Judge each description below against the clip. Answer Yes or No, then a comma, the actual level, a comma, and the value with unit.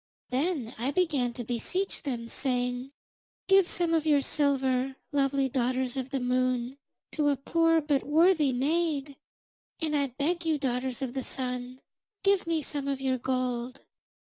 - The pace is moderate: Yes, average, 155 wpm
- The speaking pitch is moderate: No, very high, 270 Hz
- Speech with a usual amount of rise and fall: Yes, average, 3.3 semitones